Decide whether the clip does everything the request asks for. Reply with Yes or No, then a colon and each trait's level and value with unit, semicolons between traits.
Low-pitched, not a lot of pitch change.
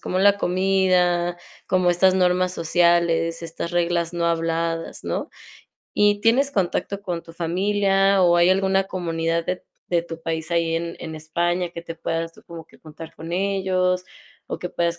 No: medium, 175 Hz; narrow, 1.9 semitones